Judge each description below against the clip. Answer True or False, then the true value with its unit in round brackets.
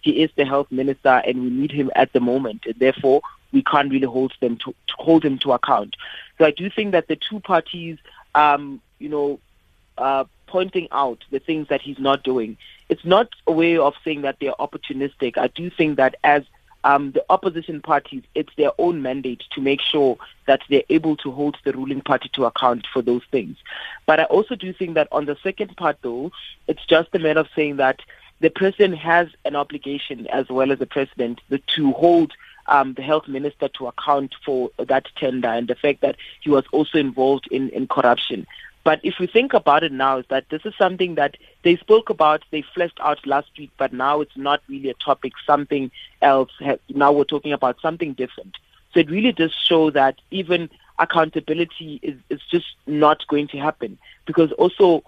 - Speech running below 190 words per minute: False (205 wpm)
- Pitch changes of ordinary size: True (3.4 semitones)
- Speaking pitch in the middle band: True (145 Hz)